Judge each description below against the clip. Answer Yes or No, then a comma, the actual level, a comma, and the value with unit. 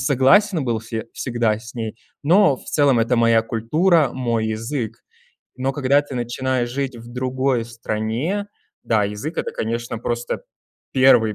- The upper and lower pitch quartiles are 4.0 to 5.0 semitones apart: No, average, 3.1 semitones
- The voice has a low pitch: Yes, low, 120 Hz